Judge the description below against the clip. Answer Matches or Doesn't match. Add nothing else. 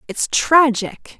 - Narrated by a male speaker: Doesn't match